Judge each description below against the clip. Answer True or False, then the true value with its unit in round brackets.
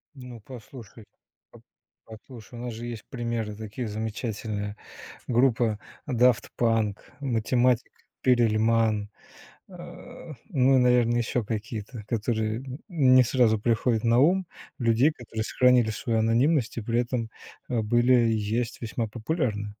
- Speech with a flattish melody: True (2.3 semitones)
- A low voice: True (115 Hz)